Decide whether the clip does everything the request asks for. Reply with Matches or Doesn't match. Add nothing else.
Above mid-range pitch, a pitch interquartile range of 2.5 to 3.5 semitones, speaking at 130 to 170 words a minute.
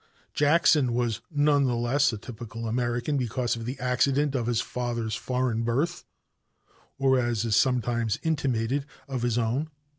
Doesn't match